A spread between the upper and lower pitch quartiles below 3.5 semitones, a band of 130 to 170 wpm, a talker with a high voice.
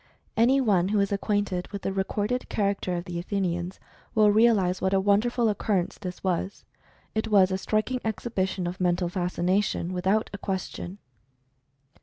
Yes: average, 2.7 semitones; average, 165 wpm; high, 195 Hz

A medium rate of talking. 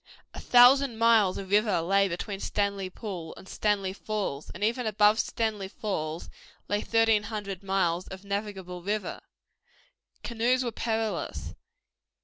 No: slow, 130 wpm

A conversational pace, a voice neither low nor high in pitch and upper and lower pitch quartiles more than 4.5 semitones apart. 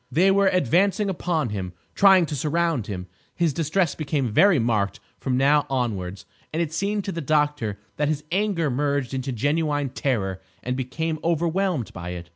Yes: average, 170 wpm; medium, 150 Hz; wide, 5.6 semitones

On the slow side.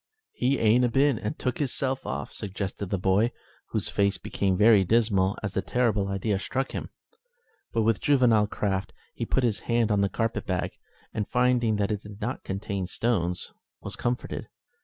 No: average, 180 wpm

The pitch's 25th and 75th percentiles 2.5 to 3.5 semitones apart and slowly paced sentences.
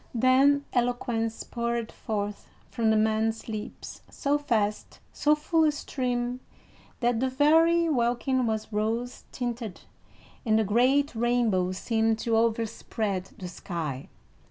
Yes: average, 2.9 semitones; slow, 125 wpm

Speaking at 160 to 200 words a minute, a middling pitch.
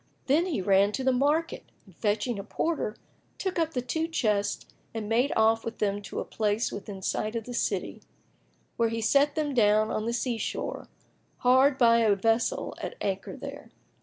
No: average, 190 wpm; high, 225 Hz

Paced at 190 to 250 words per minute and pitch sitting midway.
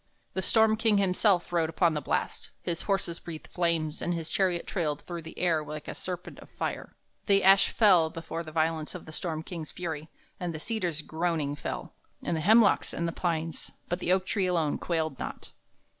Yes: average, 200 wpm; medium, 170 Hz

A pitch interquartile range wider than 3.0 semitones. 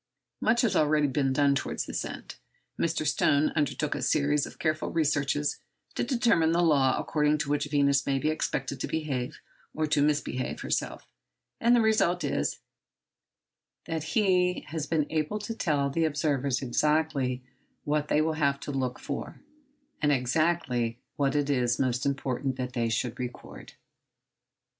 No: average, 2.7 semitones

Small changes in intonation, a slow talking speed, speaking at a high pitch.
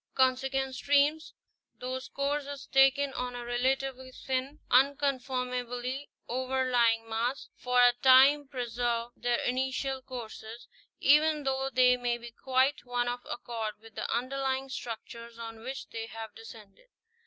Yes: narrow, 2.1 semitones; slow, 130 wpm; very high, 255 Hz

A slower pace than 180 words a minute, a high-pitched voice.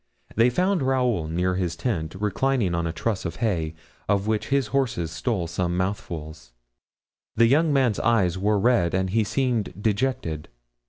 No: average, 160 wpm; low, 105 Hz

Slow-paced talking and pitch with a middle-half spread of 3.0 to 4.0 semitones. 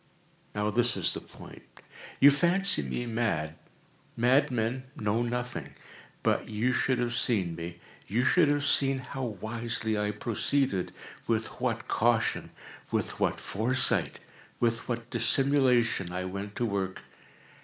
Yes: slow, 120 wpm; average, 3.7 semitones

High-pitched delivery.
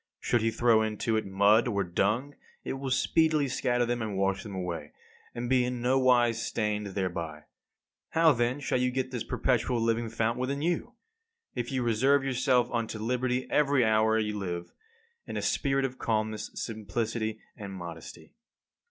No: low, 115 Hz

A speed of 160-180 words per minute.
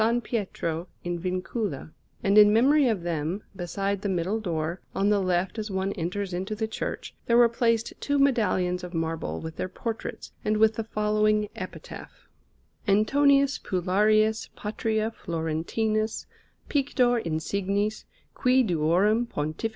No: slow, 135 wpm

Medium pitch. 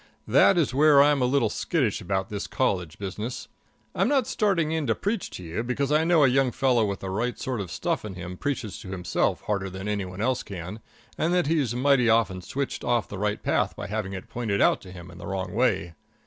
No: low, 110 Hz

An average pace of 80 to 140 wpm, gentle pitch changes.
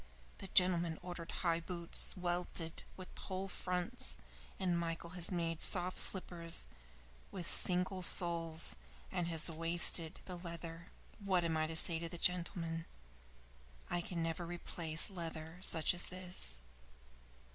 Yes: slow, 135 wpm; narrow, 1.4 semitones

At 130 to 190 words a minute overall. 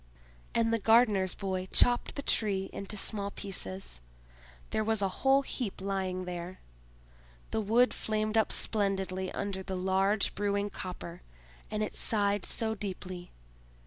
Yes: average, 140 wpm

